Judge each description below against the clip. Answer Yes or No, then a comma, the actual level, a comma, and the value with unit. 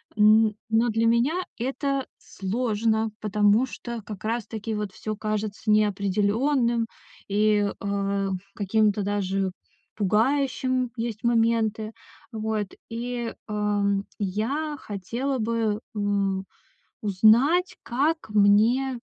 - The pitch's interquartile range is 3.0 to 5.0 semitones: No, narrow, 2.6 semitones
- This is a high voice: Yes, high, 220 Hz